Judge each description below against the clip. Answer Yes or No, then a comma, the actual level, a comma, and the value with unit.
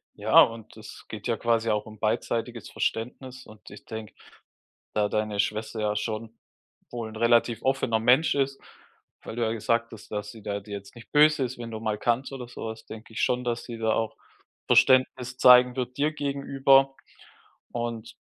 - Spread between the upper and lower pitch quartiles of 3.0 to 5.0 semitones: No, narrow, 2.5 semitones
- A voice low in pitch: Yes, low, 115 Hz